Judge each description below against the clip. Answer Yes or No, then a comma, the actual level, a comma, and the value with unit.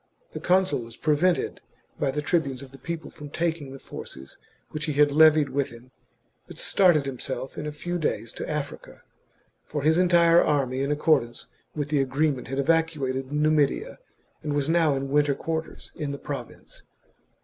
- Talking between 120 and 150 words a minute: No, average, 170 wpm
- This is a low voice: No, medium, 145 Hz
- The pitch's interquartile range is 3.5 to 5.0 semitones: No, average, 2.7 semitones